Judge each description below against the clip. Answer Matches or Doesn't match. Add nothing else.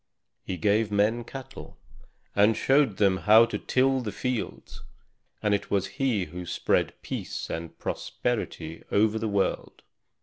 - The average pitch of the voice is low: Matches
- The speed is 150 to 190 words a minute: Doesn't match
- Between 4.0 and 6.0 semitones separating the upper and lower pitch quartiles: Doesn't match